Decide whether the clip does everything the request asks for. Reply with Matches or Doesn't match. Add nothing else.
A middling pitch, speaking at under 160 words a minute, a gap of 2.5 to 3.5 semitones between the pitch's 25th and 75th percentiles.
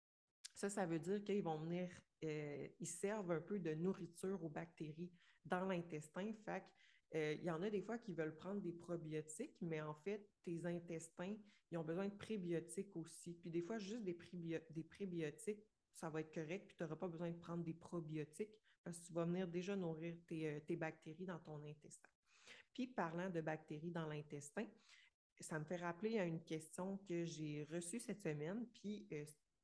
Doesn't match